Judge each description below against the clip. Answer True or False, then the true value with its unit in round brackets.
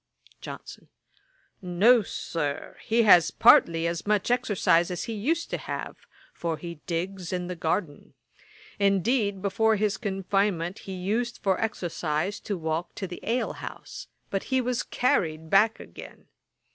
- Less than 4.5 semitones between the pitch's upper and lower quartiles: True (4.1 semitones)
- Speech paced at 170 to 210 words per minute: False (145 wpm)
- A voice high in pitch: True (195 Hz)